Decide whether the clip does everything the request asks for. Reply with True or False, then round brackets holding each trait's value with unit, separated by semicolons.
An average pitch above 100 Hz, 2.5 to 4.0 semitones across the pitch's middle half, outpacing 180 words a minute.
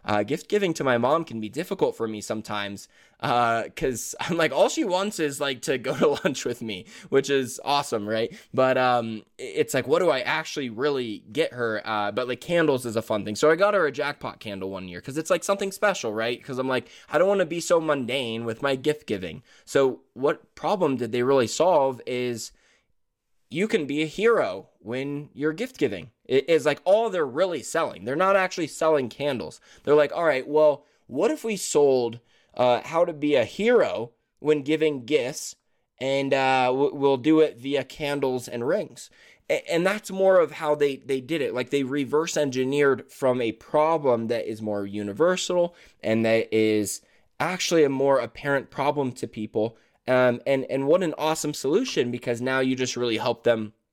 False (140 Hz; 4.7 semitones; 200 wpm)